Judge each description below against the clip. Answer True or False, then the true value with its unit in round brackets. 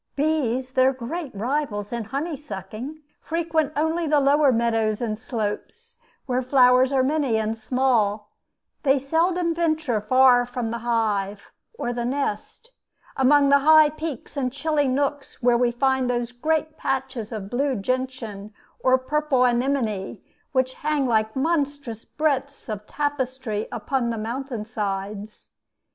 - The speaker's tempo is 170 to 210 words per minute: False (140 wpm)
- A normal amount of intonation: True (4.0 semitones)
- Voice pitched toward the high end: True (260 Hz)